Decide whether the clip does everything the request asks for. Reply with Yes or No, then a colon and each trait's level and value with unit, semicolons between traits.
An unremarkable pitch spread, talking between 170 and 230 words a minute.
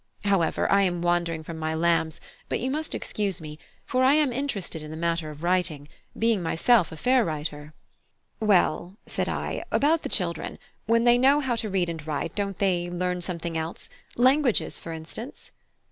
No: wide, 6.1 semitones; average, 180 wpm